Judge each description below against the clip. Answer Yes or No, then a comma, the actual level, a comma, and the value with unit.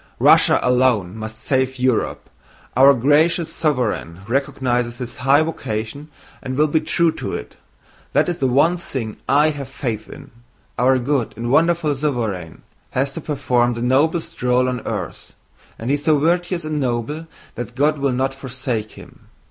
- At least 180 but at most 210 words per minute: No, average, 165 wpm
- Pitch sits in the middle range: No, low, 130 Hz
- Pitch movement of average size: Yes, average, 3.6 semitones